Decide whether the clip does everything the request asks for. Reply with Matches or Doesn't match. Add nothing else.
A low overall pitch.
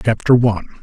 Matches